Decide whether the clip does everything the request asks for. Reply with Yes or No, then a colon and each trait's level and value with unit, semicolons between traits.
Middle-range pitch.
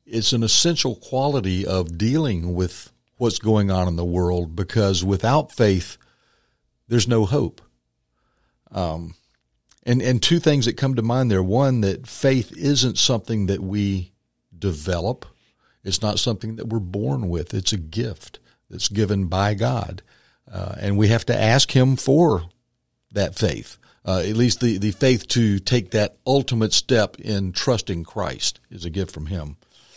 No: low, 105 Hz